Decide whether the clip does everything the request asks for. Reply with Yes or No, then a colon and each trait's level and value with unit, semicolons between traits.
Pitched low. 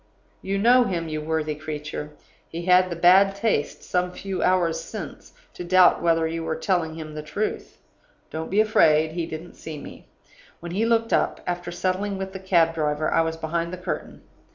No: medium, 170 Hz